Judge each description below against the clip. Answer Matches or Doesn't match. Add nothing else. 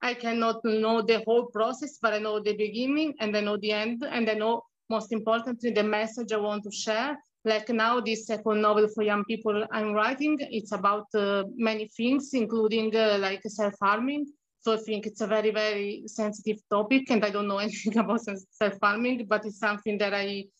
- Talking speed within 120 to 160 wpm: Doesn't match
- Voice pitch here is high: Matches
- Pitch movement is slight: Matches